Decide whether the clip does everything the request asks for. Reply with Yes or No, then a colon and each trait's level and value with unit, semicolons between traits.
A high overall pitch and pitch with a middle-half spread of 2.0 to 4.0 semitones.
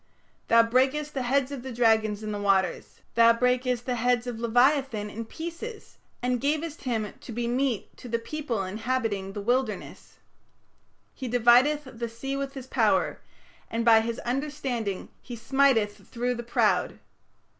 Yes: high, 245 Hz; average, 2.9 semitones